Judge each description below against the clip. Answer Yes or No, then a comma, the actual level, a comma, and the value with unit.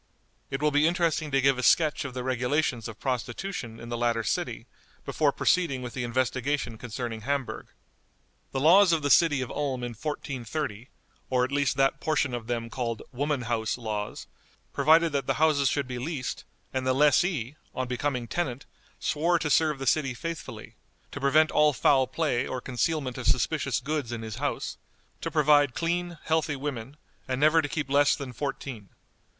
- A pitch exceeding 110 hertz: Yes, low, 135 Hz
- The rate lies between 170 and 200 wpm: Yes, average, 180 wpm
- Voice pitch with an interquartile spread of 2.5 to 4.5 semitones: Yes, average, 3.6 semitones